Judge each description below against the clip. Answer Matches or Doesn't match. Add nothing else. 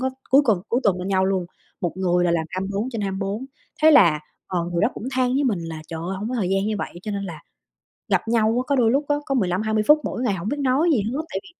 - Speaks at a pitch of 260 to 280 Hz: Doesn't match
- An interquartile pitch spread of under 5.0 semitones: Doesn't match